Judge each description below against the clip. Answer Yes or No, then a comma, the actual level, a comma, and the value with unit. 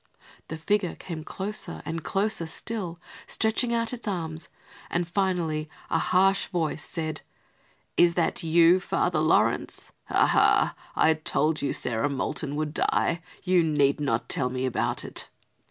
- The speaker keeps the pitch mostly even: No, average, 3.4 semitones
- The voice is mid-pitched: Yes, medium, 165 Hz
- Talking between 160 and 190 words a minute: No, average, 145 wpm